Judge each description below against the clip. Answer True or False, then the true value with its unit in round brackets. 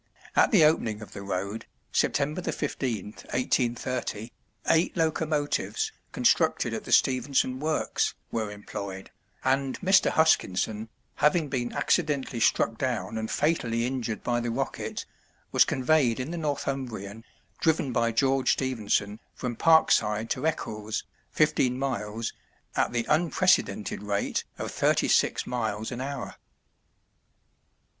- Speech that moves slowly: True (120 wpm)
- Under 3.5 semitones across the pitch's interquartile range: False (4.8 semitones)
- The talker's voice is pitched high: False (125 Hz)